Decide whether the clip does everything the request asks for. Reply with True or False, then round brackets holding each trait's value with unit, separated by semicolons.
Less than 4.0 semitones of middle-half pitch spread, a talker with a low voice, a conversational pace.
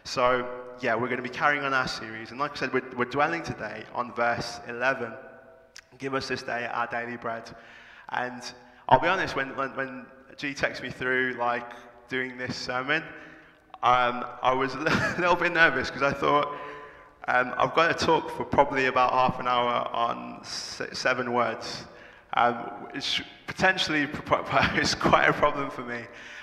True (2.4 semitones; 125 Hz; 170 wpm)